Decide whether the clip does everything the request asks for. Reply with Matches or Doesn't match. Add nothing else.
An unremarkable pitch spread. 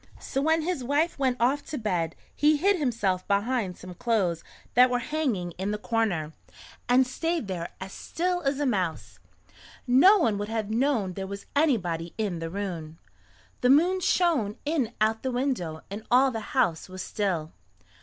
Doesn't match